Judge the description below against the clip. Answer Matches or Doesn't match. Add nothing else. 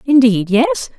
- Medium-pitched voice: Doesn't match